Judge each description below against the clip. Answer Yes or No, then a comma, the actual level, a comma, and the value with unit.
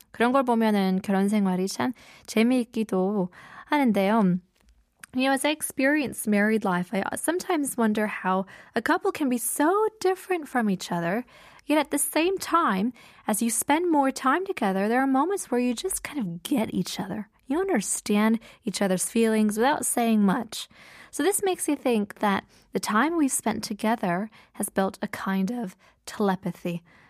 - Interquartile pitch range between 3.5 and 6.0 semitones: No, wide, 6.5 semitones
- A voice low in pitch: No, high, 225 Hz